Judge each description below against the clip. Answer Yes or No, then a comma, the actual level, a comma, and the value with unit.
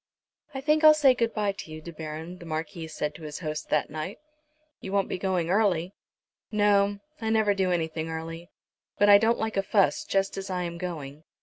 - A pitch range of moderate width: Yes, average, 4.2 semitones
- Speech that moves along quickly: Yes, fast, 210 wpm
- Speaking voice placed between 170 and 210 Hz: Yes, medium, 185 Hz